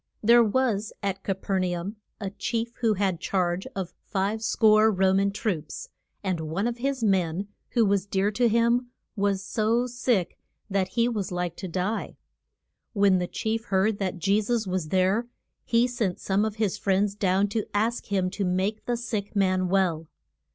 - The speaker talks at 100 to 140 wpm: No, average, 180 wpm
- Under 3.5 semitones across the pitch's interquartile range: Yes, average, 3.0 semitones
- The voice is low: No, high, 200 Hz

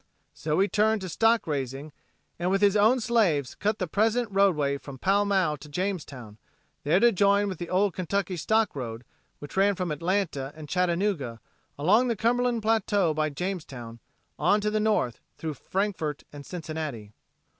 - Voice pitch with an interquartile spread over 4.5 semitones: Yes, wide, 5.6 semitones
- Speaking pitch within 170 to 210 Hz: Yes, medium, 185 Hz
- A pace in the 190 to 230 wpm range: No, average, 165 wpm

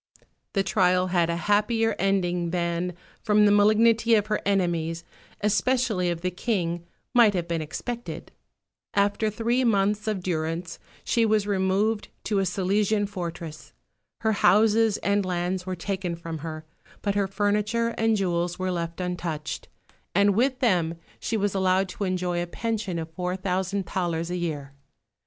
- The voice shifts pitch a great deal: No, average, 3.3 semitones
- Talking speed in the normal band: Yes, average, 155 wpm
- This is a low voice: No, high, 190 Hz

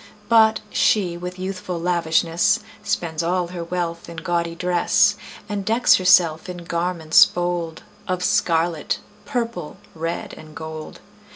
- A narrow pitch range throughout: Yes, narrow, 1.7 semitones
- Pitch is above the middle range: No, medium, 175 Hz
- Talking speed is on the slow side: Yes, slow, 125 wpm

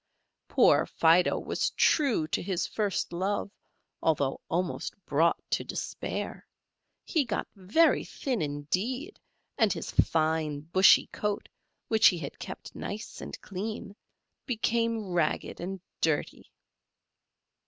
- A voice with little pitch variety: No, average, 5.3 semitones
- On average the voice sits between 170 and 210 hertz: Yes, high, 190 Hz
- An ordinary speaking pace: No, slow, 115 wpm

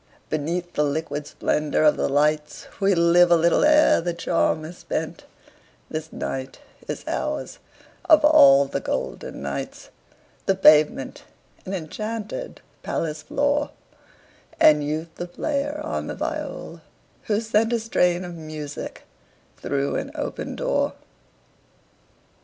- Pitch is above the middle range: No, medium, 170 Hz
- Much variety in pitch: Yes, wide, 5.9 semitones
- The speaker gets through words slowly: Yes, slow, 130 wpm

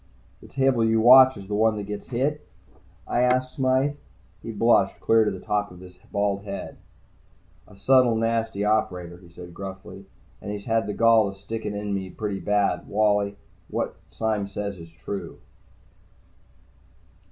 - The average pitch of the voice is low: Yes, low, 105 Hz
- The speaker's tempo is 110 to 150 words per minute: No, average, 165 wpm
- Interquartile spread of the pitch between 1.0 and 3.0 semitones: Yes, narrow, 2.5 semitones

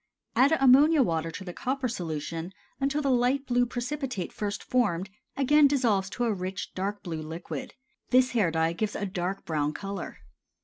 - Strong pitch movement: Yes, wide, 6.7 semitones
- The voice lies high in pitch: Yes, high, 205 Hz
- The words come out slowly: No, average, 170 wpm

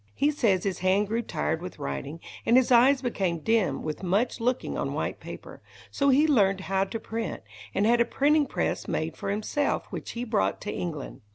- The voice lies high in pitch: Yes, high, 215 Hz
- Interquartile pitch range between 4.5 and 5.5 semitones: Yes, average, 4.9 semitones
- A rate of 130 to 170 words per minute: No, average, 200 wpm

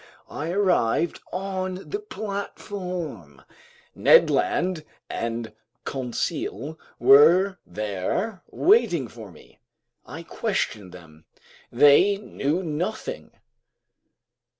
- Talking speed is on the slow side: Yes, slow, 80 wpm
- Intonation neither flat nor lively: No, wide, 8.7 semitones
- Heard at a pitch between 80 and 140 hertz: No, medium, 165 Hz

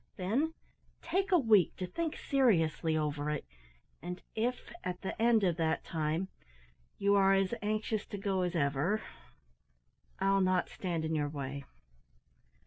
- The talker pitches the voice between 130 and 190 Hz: Yes, medium, 185 Hz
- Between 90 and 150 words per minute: Yes, average, 145 wpm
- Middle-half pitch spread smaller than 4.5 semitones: No, average, 5.2 semitones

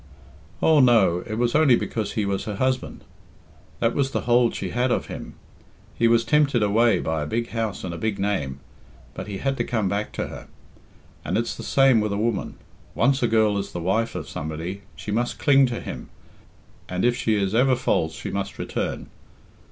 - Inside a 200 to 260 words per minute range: Yes, fast, 205 wpm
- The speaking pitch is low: Yes, low, 110 Hz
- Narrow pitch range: No, average, 3.7 semitones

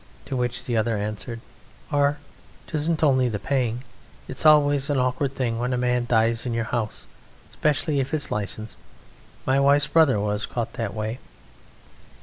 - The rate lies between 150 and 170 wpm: Yes, average, 160 wpm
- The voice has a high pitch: No, low, 125 Hz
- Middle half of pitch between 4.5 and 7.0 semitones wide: No, average, 3.8 semitones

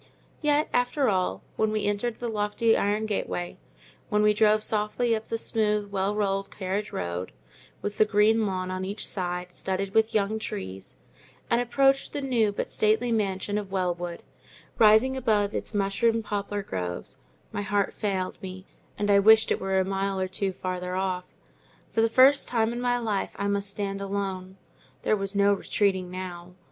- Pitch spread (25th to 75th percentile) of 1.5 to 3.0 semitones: Yes, narrow, 2.5 semitones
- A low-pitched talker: No, high, 205 Hz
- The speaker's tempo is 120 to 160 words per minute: No, average, 175 wpm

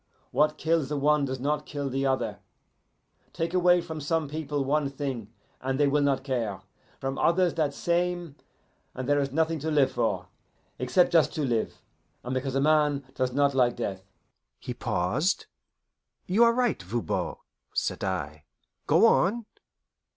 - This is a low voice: No, medium, 145 Hz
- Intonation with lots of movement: No, average, 3.5 semitones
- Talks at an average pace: Yes, average, 160 wpm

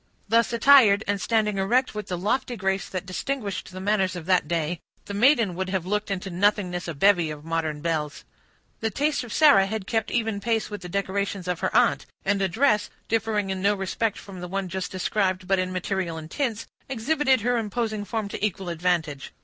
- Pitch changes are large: No, average, 3.4 semitones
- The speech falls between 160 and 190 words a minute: No, fast, 205 wpm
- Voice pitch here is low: No, high, 195 Hz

